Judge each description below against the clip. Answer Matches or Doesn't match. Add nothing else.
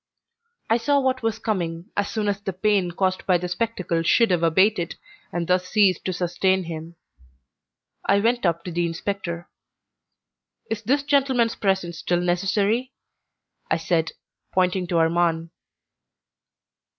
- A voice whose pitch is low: Doesn't match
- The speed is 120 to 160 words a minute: Matches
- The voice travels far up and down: Doesn't match